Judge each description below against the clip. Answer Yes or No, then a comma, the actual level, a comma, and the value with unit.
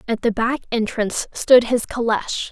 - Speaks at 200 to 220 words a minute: No, average, 165 wpm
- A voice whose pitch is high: Yes, high, 230 Hz